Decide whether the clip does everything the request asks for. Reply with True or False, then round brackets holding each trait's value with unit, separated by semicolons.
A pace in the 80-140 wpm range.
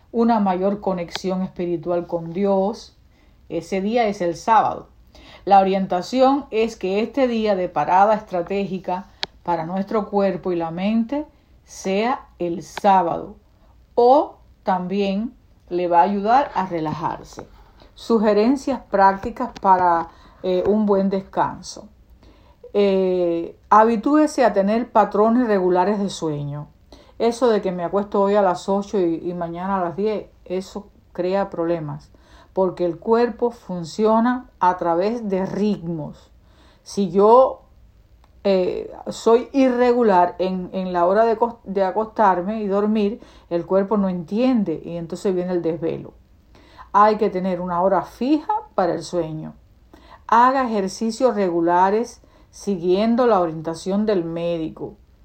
True (130 wpm)